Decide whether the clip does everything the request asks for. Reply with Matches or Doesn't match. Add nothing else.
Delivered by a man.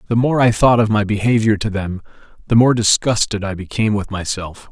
Matches